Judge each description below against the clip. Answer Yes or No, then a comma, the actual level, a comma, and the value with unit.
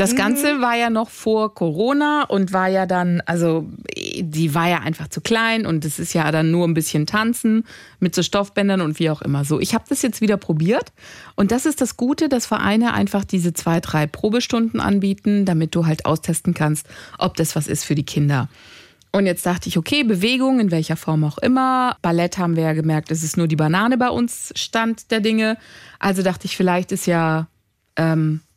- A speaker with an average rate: No, fast, 210 wpm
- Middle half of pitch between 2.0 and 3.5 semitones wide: No, wide, 5.6 semitones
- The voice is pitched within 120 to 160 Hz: No, medium, 185 Hz